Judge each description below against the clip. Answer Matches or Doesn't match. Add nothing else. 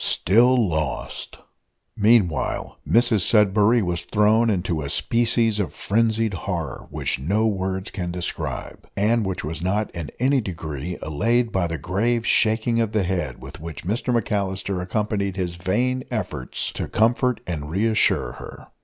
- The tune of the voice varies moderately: Matches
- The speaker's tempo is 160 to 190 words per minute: Doesn't match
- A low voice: Matches